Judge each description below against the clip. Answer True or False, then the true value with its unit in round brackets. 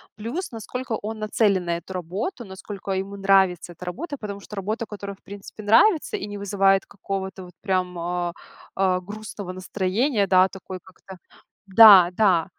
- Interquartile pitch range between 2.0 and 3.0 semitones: True (2.5 semitones)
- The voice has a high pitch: True (195 Hz)